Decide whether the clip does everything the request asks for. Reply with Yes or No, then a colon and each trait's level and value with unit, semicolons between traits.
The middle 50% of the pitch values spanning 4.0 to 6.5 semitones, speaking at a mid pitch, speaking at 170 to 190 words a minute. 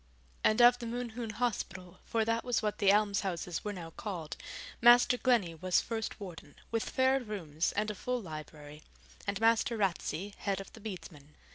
No: average, 4.6 semitones; high, 210 Hz; average, 175 wpm